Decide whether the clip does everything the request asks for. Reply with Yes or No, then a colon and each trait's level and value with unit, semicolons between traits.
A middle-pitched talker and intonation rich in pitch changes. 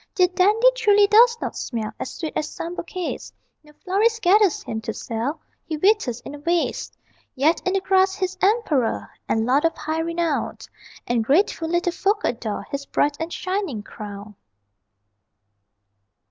No: very high, 335 Hz; wide, 6.0 semitones